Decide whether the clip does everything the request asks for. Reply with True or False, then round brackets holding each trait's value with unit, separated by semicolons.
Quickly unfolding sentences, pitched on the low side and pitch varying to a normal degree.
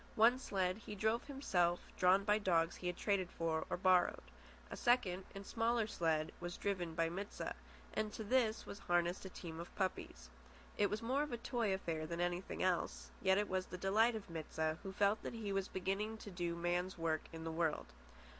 False (210 wpm; 190 Hz; 3.6 semitones)